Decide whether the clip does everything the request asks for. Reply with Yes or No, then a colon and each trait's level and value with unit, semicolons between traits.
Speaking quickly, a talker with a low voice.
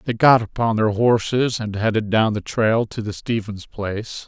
No: average, 195 wpm; low, 110 Hz